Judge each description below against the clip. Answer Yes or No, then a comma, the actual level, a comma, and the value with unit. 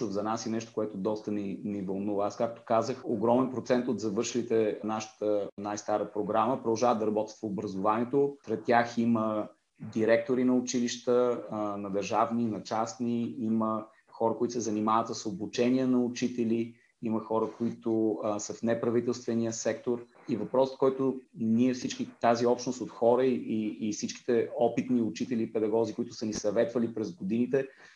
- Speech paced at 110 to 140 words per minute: No, average, 160 wpm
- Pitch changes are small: Yes, narrow, 2.0 semitones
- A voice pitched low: Yes, low, 115 Hz